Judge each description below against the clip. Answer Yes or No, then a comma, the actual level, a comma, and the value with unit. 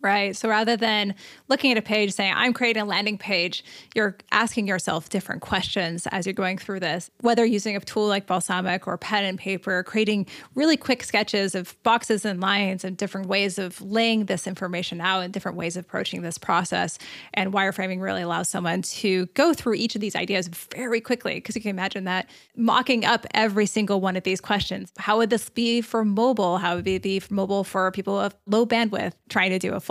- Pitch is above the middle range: Yes, high, 200 Hz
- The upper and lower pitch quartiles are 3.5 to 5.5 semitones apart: No, average, 2.7 semitones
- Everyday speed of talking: No, fast, 215 wpm